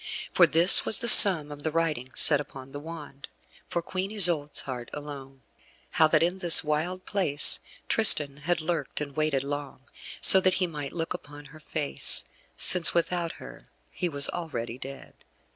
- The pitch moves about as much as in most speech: Yes, average, 3.4 semitones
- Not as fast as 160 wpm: No, average, 170 wpm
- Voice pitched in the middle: Yes, medium, 155 Hz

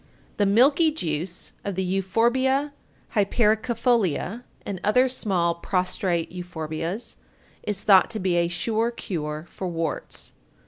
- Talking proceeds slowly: Yes, slow, 120 wpm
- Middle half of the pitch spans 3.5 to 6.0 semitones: Yes, average, 5.1 semitones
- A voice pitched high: Yes, high, 195 Hz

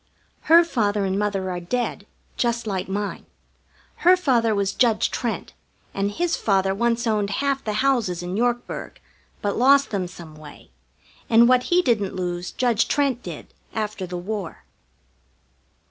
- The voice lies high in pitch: Yes, high, 215 Hz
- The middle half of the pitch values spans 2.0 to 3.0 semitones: No, average, 4.2 semitones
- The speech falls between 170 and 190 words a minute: No, average, 150 wpm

